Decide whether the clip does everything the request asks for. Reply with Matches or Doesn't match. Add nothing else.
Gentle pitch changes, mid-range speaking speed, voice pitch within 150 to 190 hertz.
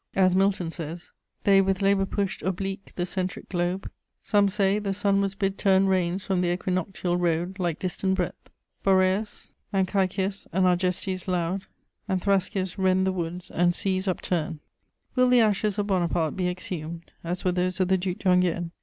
Matches